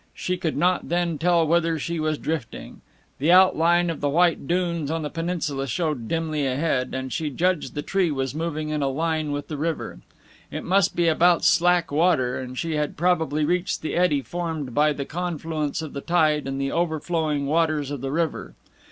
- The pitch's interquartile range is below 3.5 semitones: Yes, average, 2.9 semitones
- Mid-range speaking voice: Yes, medium, 160 Hz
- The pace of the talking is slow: No, average, 195 wpm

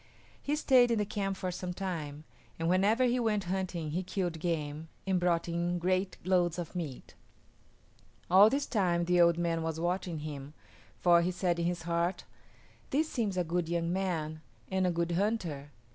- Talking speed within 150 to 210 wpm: Yes, average, 180 wpm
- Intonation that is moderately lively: No, narrow, 2.2 semitones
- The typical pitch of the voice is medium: Yes, medium, 175 Hz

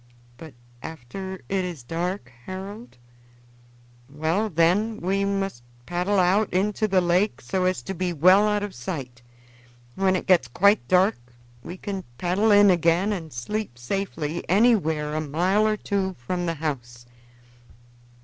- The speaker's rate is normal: Yes, average, 145 wpm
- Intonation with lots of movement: No, average, 3.9 semitones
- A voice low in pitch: No, medium, 185 Hz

